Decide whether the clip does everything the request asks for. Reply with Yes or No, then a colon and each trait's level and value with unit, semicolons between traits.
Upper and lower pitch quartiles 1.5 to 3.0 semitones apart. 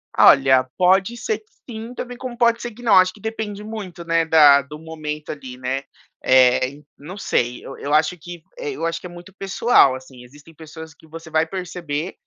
No: wide, 5.6 semitones